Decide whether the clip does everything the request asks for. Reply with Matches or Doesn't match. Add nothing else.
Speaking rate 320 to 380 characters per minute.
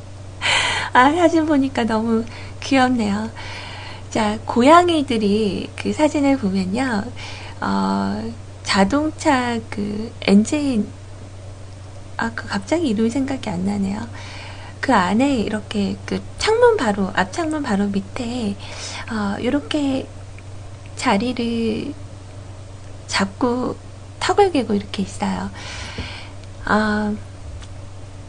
Doesn't match